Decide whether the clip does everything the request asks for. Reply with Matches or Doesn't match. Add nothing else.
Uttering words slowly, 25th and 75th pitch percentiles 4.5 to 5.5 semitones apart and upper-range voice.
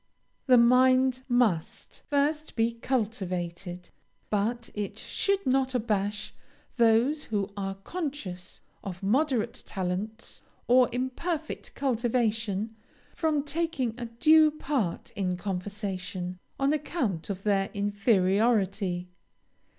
Matches